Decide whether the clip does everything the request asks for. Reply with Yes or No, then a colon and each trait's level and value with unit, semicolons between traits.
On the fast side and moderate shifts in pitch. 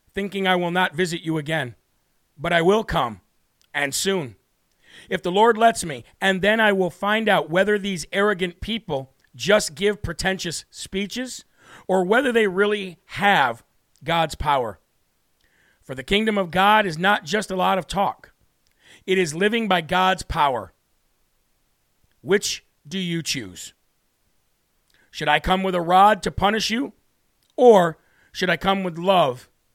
No: average, 155 wpm; average, 4.3 semitones